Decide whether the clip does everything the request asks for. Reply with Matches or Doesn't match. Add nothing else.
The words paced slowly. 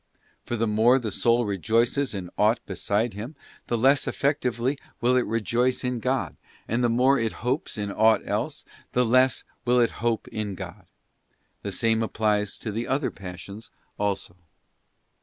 Doesn't match